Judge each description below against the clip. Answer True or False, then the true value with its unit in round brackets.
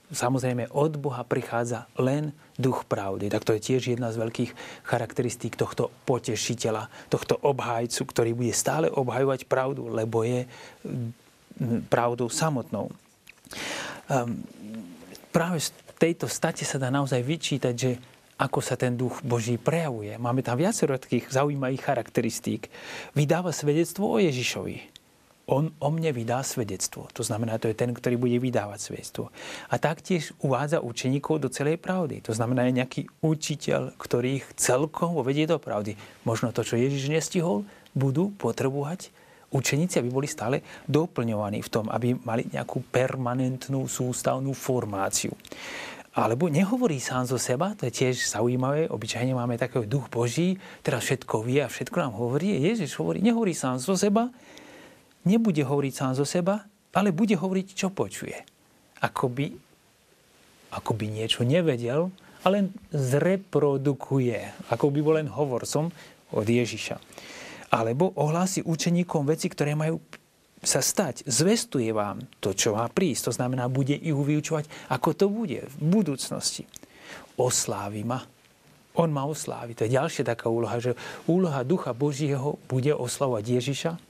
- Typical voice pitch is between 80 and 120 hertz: False (135 Hz)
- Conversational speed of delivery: True (140 wpm)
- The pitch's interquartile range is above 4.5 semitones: True (4.9 semitones)